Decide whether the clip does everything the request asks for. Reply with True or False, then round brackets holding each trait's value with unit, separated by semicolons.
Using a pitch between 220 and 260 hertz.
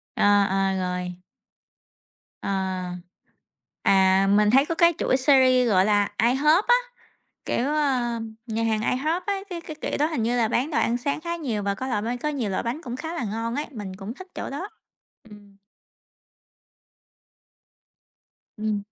True (240 Hz)